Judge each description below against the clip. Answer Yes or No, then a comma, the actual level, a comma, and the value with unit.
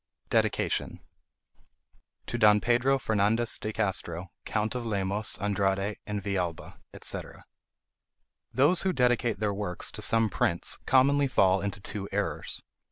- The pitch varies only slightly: No, average, 3.4 semitones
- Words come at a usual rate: No, slow, 125 wpm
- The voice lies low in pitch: Yes, low, 105 Hz